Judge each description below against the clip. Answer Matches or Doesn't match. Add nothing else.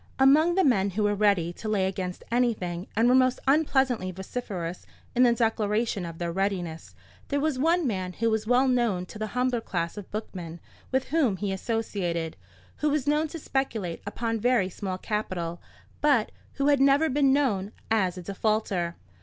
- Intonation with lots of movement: Matches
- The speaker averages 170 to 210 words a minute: Matches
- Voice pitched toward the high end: Matches